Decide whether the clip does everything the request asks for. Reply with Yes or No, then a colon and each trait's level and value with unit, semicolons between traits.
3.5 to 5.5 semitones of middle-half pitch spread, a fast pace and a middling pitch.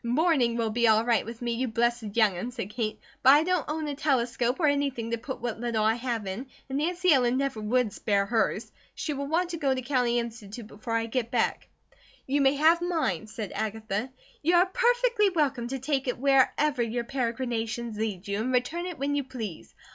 No: average, 4.0 semitones; fast, 210 wpm; high, 245 Hz